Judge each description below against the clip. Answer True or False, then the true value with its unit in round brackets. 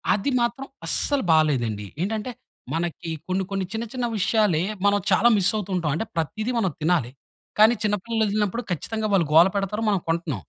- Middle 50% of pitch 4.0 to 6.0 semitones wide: True (4.8 semitones)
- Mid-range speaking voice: False (195 Hz)